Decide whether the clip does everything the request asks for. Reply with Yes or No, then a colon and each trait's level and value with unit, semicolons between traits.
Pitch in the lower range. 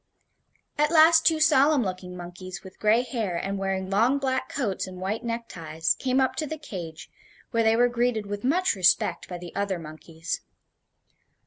No: high, 210 Hz